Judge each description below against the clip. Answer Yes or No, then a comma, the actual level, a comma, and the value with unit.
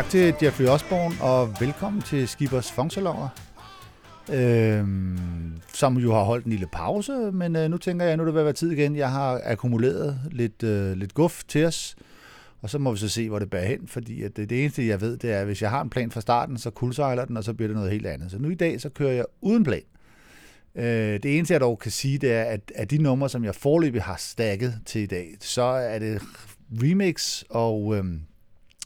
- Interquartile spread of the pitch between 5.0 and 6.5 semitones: Yes, wide, 5.4 semitones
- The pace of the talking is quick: Yes, fast, 230 wpm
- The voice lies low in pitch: Yes, low, 125 Hz